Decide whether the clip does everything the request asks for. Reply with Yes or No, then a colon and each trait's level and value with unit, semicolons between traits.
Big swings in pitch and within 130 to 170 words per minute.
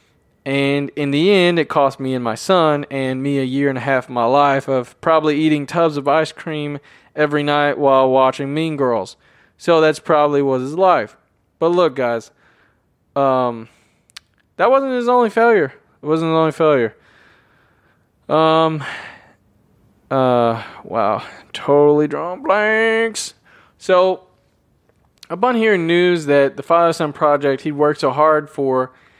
No: average, 3.1 semitones; average, 150 wpm